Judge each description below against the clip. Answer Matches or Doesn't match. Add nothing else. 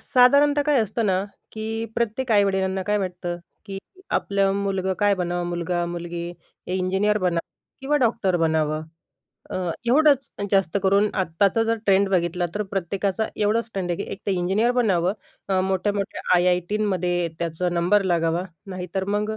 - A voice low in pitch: Doesn't match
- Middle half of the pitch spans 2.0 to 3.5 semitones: Matches